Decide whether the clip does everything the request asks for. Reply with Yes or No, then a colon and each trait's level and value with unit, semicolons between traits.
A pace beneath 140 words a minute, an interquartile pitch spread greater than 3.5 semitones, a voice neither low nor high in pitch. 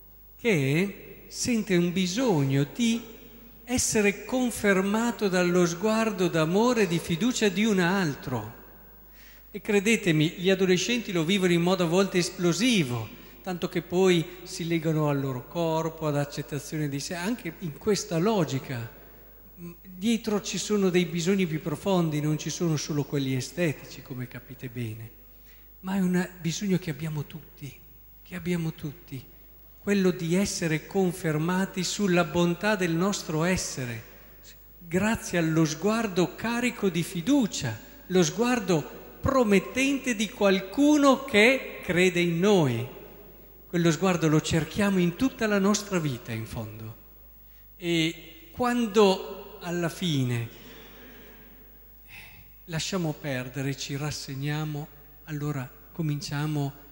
Yes: average, 120 wpm; average, 5.2 semitones; medium, 175 Hz